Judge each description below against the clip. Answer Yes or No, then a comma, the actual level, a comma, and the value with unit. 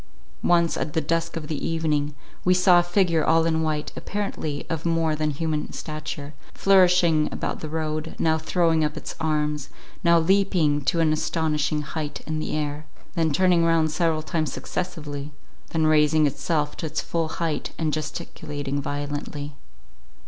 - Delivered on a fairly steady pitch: Yes, narrow, 1.7 semitones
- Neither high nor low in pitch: Yes, medium, 155 Hz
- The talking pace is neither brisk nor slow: Yes, average, 160 wpm